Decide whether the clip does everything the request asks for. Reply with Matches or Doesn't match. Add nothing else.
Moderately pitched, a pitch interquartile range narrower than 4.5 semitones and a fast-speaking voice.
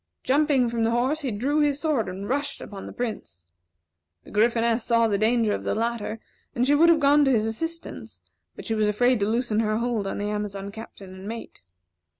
Doesn't match